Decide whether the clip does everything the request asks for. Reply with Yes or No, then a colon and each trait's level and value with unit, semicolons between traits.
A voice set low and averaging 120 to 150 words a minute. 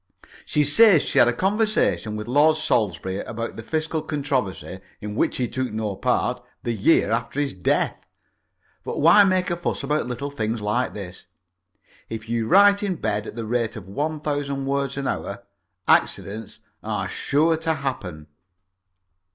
No: low, 130 Hz; average, 165 wpm